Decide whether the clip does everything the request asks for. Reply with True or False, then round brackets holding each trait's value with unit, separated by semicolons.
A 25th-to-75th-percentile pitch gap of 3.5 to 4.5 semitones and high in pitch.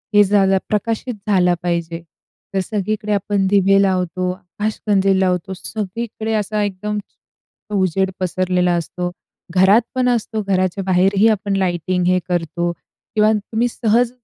False (2.5 semitones; 195 Hz)